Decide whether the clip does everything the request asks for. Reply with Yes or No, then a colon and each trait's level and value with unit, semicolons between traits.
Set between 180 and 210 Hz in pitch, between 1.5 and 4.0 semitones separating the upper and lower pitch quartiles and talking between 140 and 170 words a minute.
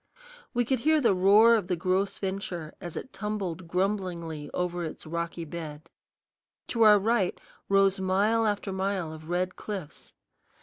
Yes: high, 190 Hz; average, 3.5 semitones; average, 150 wpm